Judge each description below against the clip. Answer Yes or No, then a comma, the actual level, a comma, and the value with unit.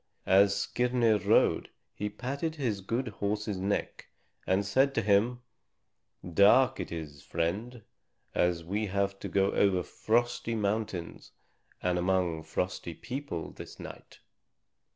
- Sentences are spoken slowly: Yes, slow, 125 wpm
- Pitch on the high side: No, low, 100 Hz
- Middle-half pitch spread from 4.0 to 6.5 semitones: Yes, average, 4.3 semitones